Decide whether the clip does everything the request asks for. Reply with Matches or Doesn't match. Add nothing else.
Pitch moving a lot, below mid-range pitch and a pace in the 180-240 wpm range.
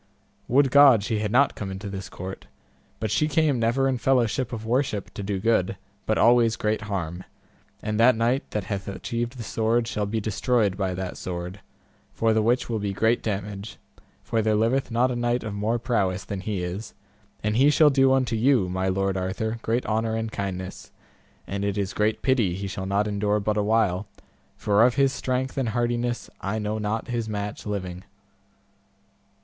Doesn't match